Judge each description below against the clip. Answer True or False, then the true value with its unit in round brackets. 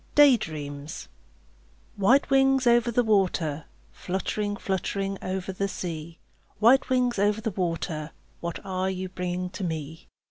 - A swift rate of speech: False (135 wpm)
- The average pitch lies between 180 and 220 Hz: True (190 Hz)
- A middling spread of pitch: True (4.5 semitones)